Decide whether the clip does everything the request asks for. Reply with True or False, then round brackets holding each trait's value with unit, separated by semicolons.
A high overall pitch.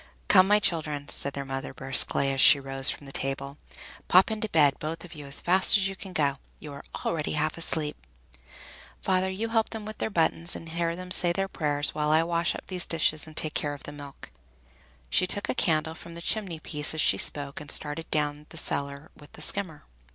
False (155 Hz)